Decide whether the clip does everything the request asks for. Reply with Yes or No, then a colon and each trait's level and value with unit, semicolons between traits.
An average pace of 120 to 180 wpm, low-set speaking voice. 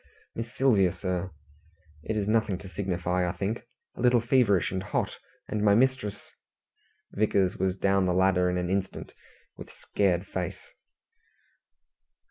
Yes: average, 145 wpm; very low, 95 Hz